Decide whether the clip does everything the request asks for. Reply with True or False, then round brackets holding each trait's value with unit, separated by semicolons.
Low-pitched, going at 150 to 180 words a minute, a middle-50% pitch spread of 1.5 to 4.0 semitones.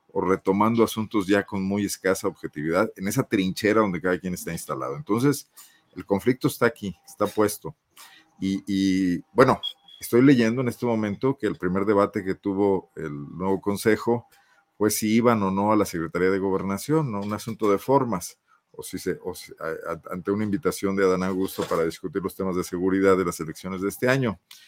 False (100 Hz; 190 wpm; 2.8 semitones)